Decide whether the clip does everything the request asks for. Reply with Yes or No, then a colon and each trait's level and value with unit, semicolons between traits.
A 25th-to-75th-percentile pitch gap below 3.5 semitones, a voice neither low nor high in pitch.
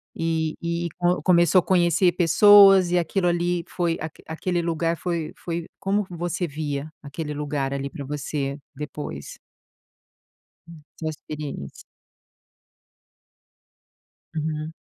Yes: average, 2.7 semitones; medium, 165 Hz